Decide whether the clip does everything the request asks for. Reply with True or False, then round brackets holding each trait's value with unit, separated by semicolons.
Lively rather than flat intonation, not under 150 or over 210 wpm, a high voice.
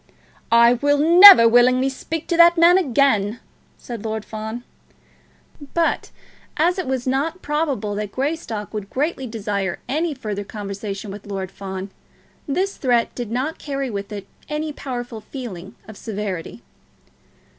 False (6.0 semitones; 140 wpm; 240 Hz)